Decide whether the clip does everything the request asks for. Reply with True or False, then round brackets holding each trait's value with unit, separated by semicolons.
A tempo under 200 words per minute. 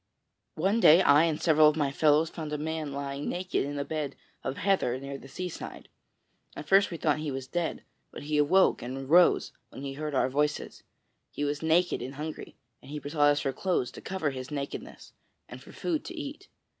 False (205 wpm)